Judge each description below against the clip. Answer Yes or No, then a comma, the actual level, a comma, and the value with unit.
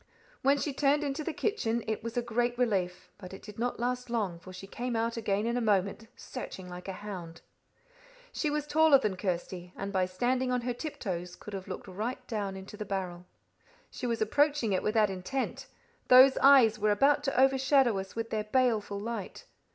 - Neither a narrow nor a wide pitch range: Yes, average, 4.7 semitones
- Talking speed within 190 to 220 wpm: Yes, average, 200 wpm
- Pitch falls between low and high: No, high, 225 Hz